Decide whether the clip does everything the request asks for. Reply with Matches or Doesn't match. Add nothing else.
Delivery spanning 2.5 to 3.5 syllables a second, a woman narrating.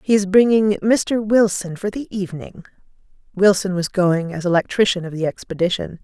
Matches